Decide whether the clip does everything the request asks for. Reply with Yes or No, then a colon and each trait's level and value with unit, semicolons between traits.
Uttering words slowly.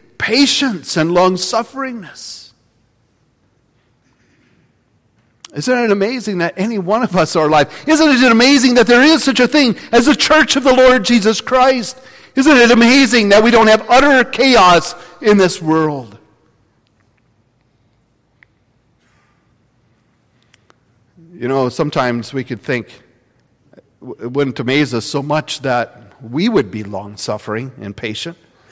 Yes: slow, 125 wpm